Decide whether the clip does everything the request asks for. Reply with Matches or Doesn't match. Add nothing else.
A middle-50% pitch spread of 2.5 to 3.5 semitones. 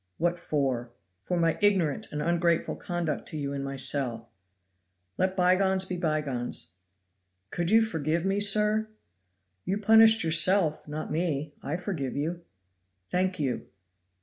Doesn't match